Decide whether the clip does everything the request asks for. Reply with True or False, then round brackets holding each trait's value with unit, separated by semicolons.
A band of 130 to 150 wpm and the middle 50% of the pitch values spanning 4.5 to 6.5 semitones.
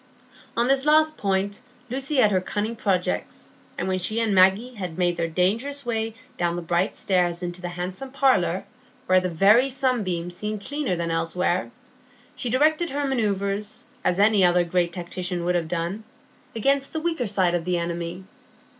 False (170 wpm; 5.5 semitones)